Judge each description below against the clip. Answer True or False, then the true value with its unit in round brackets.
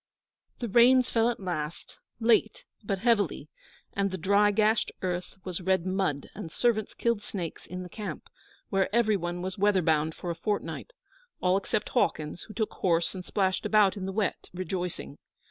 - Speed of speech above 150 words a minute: True (175 wpm)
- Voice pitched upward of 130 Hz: True (190 Hz)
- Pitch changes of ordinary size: True (3.1 semitones)